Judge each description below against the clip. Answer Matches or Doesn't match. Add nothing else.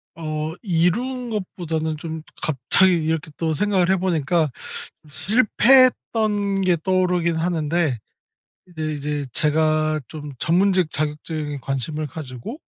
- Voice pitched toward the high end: Doesn't match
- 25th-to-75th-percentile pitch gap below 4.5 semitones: Matches